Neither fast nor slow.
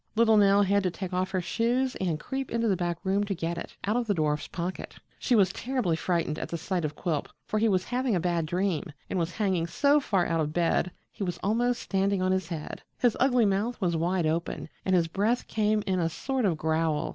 No: fast, 240 wpm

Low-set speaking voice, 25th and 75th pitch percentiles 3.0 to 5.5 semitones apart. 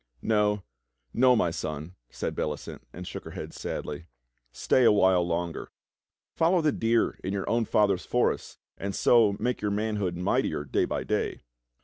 Yes: low, 100 Hz; average, 4.5 semitones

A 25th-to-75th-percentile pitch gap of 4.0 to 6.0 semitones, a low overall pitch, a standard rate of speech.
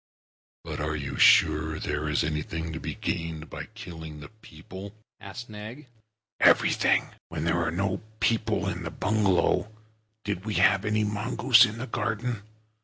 Yes: average, 5.3 semitones; low, 100 Hz; average, 160 wpm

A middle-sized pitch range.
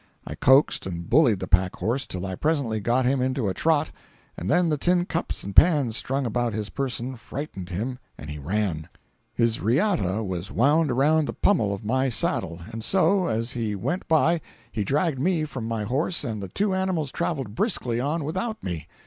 No: wide, 7.0 semitones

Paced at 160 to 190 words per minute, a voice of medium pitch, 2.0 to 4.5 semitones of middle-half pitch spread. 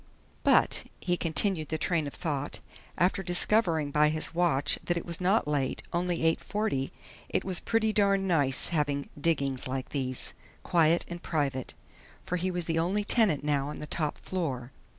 Yes: average, 170 wpm; medium, 165 Hz; average, 3.8 semitones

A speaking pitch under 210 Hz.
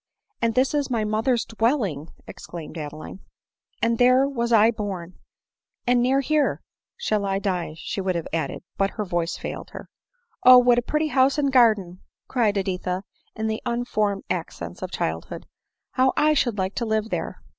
No: high, 220 Hz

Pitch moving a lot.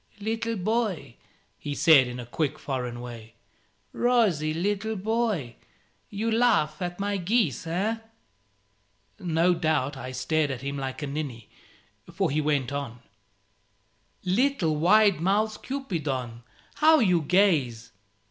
Yes: wide, 7.4 semitones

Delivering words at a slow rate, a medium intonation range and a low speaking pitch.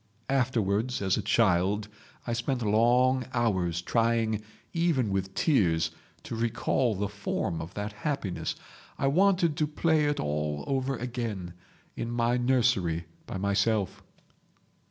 Yes: slow, 120 wpm; average, 4.9 semitones; low, 115 Hz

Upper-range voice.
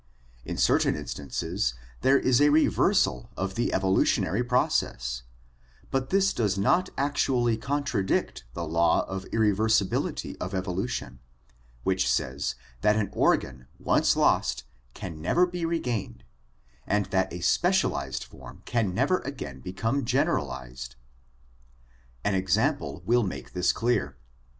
No: low, 100 Hz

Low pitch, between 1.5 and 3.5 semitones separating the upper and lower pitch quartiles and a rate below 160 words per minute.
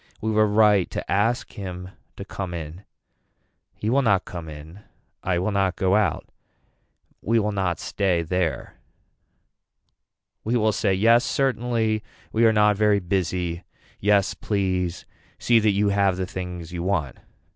Yes: low, 100 Hz; average, 3.0 semitones; average, 150 wpm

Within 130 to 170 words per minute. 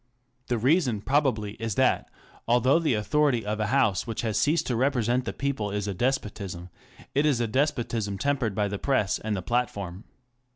No: average, 180 wpm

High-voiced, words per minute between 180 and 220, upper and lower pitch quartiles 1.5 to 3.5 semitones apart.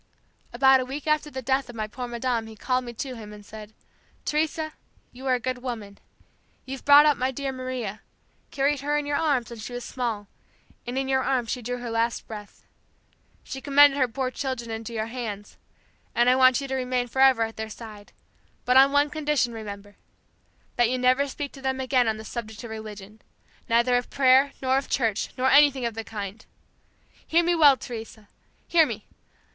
Yes: very high, 250 Hz; average, 200 wpm; average, 3.1 semitones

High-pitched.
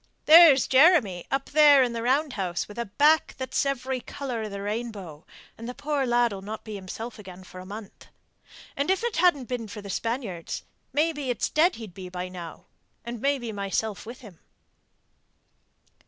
Yes: high, 235 Hz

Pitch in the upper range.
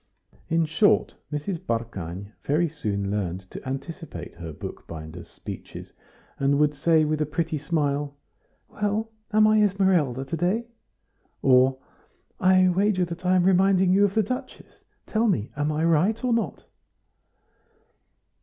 No: medium, 160 Hz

